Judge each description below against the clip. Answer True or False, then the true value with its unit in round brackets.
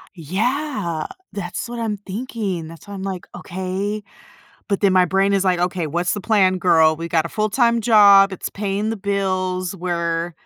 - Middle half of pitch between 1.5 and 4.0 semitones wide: True (2.8 semitones)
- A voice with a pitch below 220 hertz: True (190 Hz)